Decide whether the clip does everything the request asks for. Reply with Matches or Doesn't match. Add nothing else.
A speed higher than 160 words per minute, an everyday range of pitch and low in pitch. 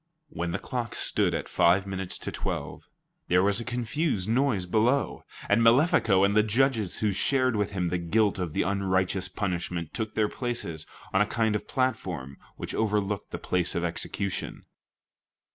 Matches